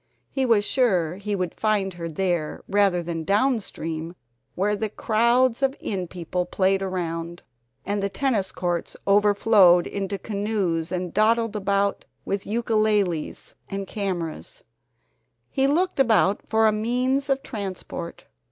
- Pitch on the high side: Yes, high, 200 Hz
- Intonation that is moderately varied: Yes, average, 3.8 semitones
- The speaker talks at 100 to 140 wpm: Yes, slow, 135 wpm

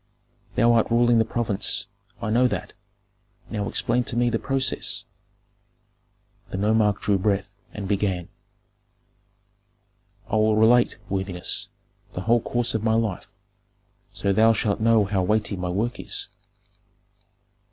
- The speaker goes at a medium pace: No, slow, 130 wpm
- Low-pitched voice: Yes, low, 110 Hz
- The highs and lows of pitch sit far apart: No, average, 2.7 semitones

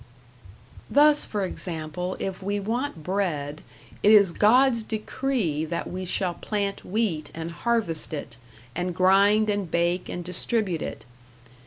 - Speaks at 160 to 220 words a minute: No, slow, 135 wpm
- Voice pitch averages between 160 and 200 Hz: Yes, high, 190 Hz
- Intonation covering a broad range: No, average, 4.1 semitones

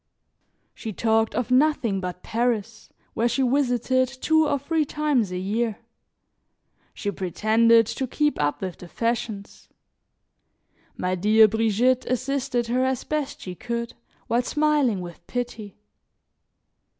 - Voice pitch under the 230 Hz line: No, high, 235 Hz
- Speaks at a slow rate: Yes, slow, 125 wpm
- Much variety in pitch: No, average, 3.5 semitones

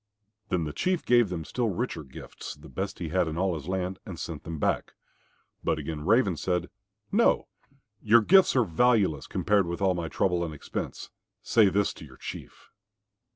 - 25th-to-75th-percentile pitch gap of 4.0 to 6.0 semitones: Yes, average, 4.7 semitones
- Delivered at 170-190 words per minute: Yes, average, 180 wpm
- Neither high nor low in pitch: No, very low, 90 Hz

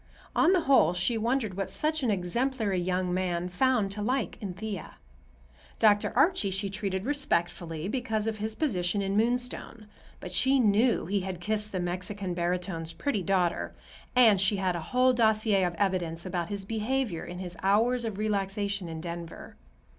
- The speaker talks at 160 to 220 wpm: Yes, average, 170 wpm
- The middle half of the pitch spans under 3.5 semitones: No, average, 4.0 semitones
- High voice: Yes, high, 200 Hz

